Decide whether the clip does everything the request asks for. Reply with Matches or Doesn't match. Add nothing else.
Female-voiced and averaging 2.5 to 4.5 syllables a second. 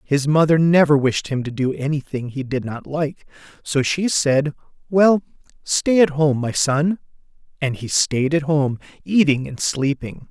Doesn't match